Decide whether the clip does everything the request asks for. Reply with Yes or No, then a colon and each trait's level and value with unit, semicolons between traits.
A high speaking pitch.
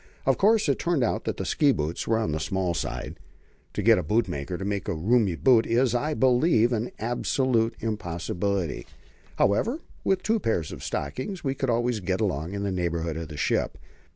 No: low, 110 Hz